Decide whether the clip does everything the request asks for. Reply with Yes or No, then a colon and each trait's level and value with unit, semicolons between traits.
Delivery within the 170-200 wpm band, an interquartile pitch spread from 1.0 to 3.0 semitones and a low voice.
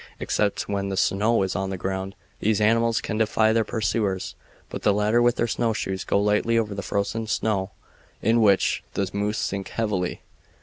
Yes: average, 180 wpm; narrow, 2.4 semitones; low, 105 Hz